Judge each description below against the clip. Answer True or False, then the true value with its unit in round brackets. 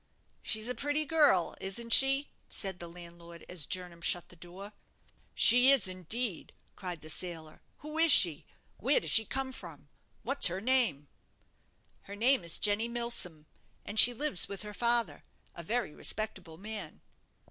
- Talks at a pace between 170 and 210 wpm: False (160 wpm)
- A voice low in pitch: False (205 Hz)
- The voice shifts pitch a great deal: True (6.1 semitones)